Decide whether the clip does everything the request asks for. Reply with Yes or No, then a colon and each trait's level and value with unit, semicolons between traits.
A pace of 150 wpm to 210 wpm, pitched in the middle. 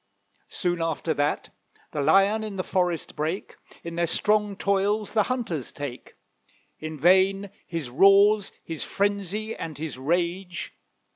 No: slow, 135 wpm; medium, 180 Hz